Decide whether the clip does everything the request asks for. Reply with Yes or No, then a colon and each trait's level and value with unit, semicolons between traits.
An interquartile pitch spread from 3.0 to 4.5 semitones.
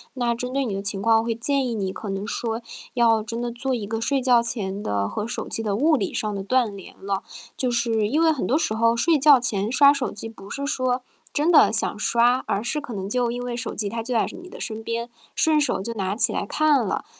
Yes: average, 3.4 semitones